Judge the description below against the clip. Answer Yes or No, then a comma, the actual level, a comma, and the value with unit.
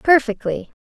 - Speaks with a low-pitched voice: No, very high, 250 Hz